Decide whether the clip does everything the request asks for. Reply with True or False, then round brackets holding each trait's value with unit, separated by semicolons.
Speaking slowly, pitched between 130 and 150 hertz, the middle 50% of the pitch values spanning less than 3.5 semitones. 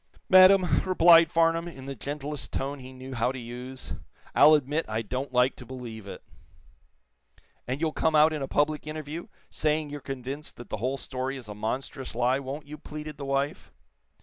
False (185 wpm; 140 Hz; 3.1 semitones)